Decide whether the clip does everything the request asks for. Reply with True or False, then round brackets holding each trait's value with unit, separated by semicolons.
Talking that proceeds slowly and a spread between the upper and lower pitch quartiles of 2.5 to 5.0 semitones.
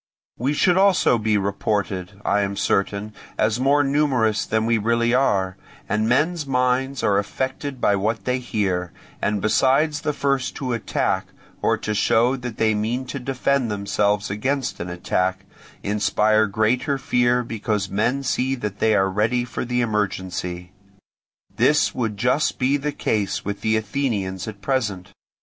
False (155 wpm; 4.2 semitones)